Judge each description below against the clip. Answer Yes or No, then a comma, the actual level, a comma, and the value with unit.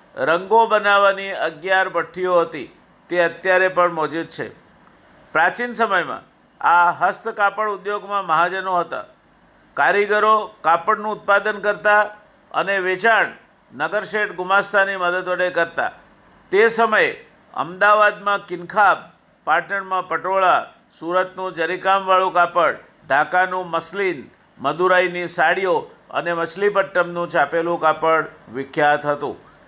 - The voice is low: No, medium, 185 Hz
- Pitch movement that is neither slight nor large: Yes, average, 3.0 semitones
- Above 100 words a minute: No, average, 95 wpm